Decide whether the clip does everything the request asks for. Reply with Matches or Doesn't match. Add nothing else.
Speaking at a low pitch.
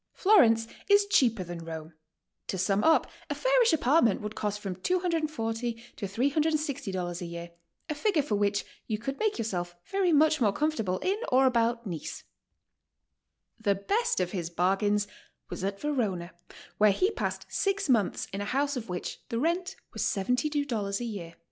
Doesn't match